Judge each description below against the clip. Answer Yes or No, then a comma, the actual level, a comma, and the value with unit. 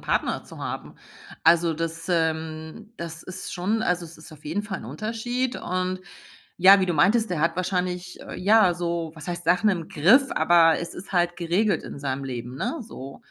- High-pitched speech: No, medium, 175 Hz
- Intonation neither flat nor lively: Yes, average, 3.0 semitones